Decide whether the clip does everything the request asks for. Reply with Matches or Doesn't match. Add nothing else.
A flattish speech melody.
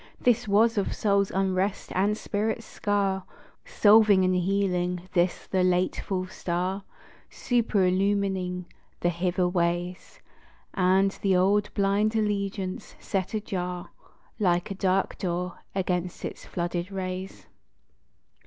Matches